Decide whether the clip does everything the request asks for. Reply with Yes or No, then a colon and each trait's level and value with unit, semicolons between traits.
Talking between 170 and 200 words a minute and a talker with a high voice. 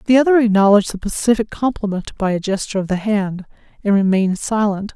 Yes: average, 180 wpm; high, 210 Hz